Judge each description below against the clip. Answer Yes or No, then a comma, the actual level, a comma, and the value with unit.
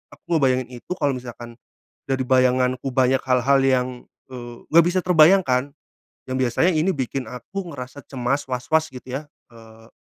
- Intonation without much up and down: Yes, narrow, 2.1 semitones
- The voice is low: Yes, low, 130 Hz